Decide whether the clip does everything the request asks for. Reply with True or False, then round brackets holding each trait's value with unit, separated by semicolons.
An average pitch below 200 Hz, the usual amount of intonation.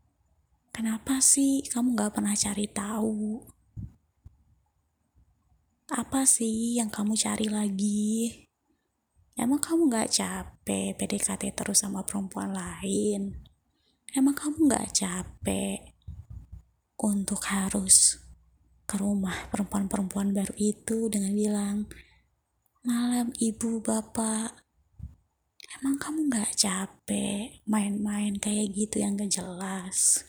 False (210 Hz; 3.0 semitones)